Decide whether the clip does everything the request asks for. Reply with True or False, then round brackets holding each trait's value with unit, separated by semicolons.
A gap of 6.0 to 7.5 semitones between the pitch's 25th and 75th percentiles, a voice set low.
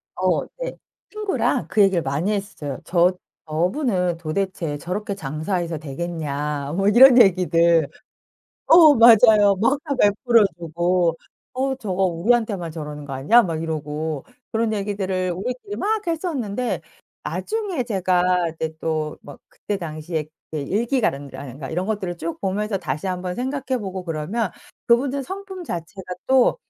False (6.5 semitones; 185 Hz)